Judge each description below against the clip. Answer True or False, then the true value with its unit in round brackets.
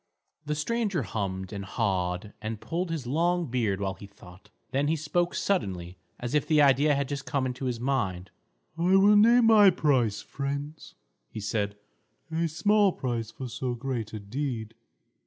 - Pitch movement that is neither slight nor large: False (7.3 semitones)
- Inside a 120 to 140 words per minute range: False (170 wpm)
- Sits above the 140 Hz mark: False (130 Hz)